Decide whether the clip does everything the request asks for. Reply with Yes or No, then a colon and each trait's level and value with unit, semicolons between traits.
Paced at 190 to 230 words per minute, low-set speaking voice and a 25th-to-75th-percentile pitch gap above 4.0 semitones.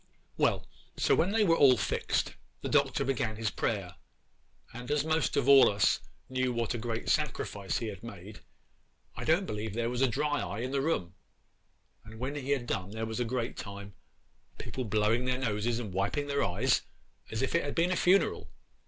Yes: average, 195 wpm; low, 120 Hz; average, 4.7 semitones